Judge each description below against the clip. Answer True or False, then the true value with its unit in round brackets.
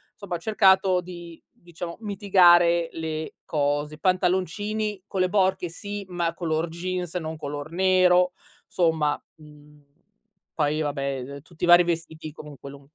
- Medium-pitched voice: True (170 Hz)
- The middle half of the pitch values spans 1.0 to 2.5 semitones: False (2.9 semitones)